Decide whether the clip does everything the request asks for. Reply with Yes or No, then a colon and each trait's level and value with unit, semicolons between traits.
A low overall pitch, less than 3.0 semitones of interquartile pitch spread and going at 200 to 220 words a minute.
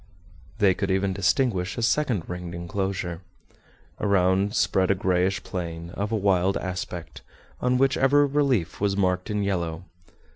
No: very low, 95 Hz; narrow, 2.6 semitones; average, 145 wpm